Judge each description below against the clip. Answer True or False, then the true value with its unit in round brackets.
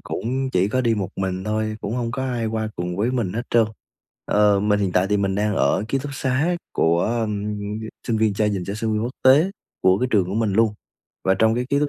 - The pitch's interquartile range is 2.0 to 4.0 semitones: True (3.3 semitones)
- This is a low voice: True (110 Hz)